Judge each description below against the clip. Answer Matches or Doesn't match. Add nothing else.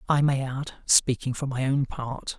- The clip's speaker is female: Doesn't match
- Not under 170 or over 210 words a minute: Matches